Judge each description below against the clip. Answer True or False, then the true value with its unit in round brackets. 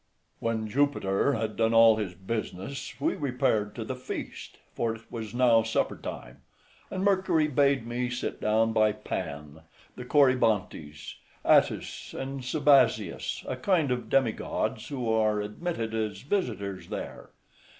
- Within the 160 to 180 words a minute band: False (140 wpm)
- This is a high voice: False (115 Hz)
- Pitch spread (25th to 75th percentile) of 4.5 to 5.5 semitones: False (4.1 semitones)